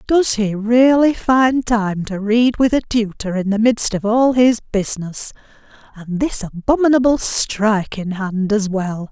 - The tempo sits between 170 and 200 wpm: No, average, 160 wpm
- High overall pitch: Yes, high, 220 Hz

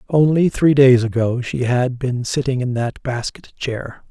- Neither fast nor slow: Yes, average, 175 wpm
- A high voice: No, low, 130 Hz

